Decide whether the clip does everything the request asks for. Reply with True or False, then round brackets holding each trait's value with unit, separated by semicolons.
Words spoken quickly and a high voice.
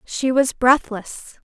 False (125 wpm; 250 Hz)